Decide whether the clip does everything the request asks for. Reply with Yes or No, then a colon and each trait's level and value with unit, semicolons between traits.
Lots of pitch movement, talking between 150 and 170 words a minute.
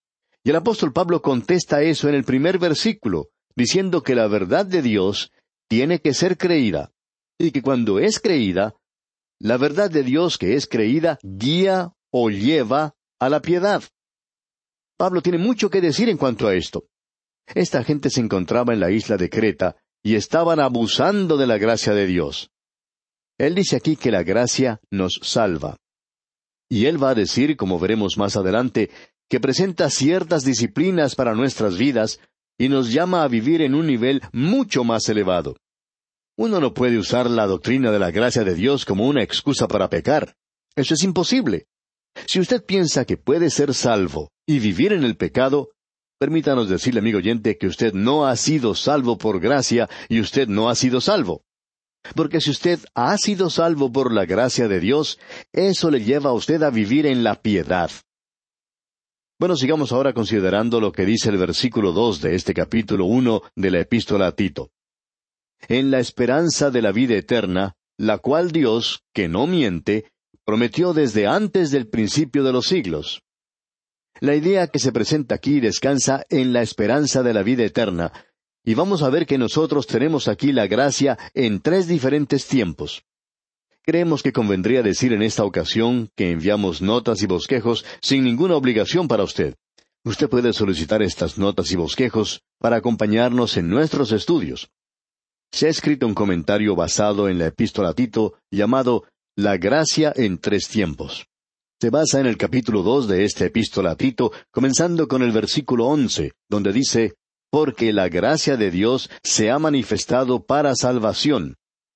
Yes: wide, 5.8 semitones; average, 165 wpm